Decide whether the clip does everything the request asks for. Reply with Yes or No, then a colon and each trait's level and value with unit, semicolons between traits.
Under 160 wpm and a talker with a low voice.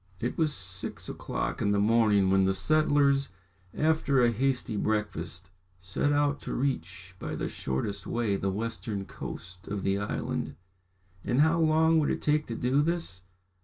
No: average, 165 wpm; low, 115 Hz